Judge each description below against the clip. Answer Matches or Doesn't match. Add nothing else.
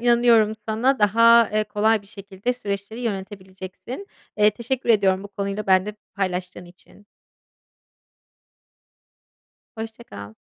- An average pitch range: Matches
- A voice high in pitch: Matches